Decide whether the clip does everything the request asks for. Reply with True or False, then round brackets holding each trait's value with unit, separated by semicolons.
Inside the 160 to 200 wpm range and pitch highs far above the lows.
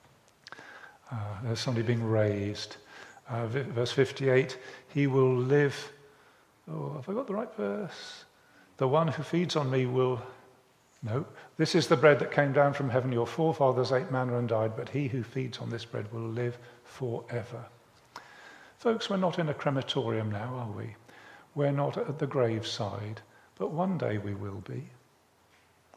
False (165 wpm; 3.7 semitones)